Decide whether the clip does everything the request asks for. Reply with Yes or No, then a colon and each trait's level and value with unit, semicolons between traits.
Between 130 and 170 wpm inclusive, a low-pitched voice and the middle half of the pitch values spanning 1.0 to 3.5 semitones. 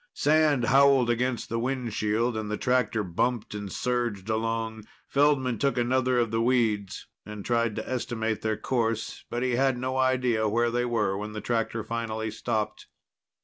Yes: average, 165 wpm; low, 115 Hz; narrow, 2.4 semitones